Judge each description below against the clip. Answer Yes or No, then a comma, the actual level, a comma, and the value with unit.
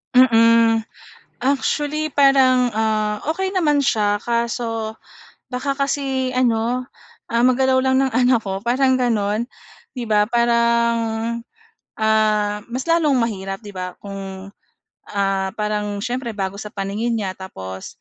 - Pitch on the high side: Yes, high, 230 Hz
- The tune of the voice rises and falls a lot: No, average, 3.7 semitones